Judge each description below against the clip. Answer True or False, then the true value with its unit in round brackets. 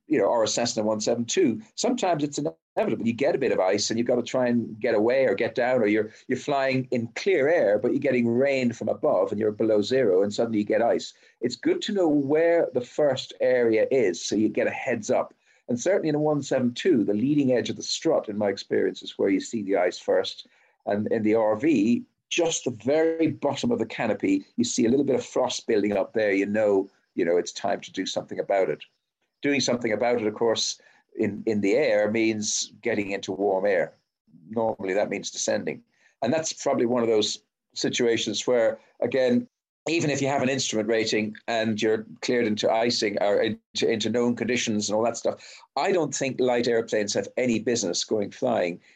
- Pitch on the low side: True (120 Hz)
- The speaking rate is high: True (215 wpm)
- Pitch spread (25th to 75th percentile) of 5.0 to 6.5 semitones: True (5.6 semitones)